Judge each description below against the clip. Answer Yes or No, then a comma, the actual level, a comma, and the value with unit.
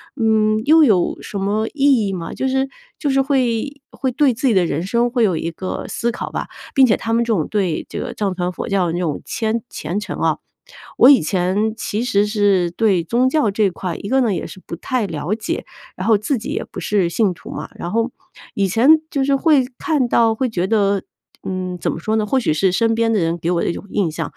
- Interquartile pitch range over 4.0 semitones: Yes, average, 4.7 semitones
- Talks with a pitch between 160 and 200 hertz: No, high, 215 Hz